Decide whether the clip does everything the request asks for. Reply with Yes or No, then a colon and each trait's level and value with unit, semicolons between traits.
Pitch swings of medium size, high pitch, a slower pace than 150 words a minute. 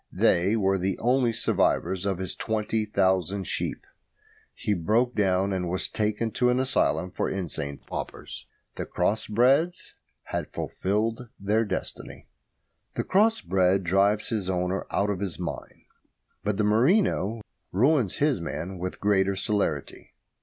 No: average, 3.2 semitones; low, 100 Hz; average, 140 wpm